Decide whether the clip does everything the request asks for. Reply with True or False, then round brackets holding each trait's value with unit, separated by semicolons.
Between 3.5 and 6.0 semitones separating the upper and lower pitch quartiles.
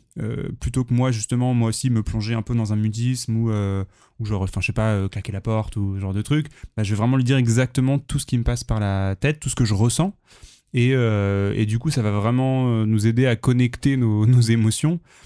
False (3.1 semitones)